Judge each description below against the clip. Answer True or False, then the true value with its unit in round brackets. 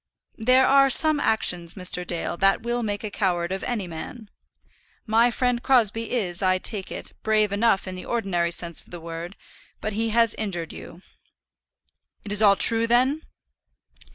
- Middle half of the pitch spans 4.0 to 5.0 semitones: True (4.4 semitones)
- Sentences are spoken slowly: False (170 wpm)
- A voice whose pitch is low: False (210 Hz)